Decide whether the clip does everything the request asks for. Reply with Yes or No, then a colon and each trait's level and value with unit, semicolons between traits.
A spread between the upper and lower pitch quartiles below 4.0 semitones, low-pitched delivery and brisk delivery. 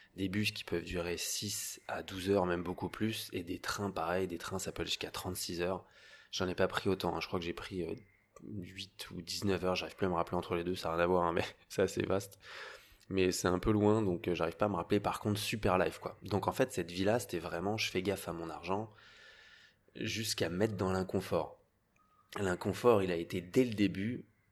Yes: average, 2.8 semitones; very low, 95 Hz; fast, 240 wpm